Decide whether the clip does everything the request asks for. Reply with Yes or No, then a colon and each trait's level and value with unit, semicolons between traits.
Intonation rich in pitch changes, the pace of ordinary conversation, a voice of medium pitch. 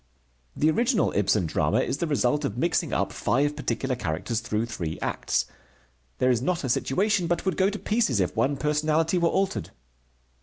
Yes: wide, 6.8 semitones; average, 180 wpm; medium, 145 Hz